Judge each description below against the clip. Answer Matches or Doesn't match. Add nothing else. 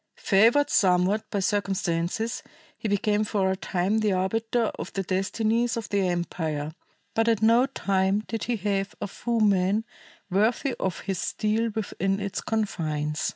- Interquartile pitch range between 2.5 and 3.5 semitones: Matches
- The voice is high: Matches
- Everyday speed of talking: Matches